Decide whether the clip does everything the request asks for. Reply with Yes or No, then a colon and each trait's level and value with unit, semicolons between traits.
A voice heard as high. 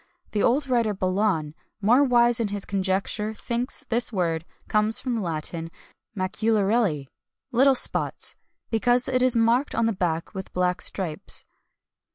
Yes: high, 215 Hz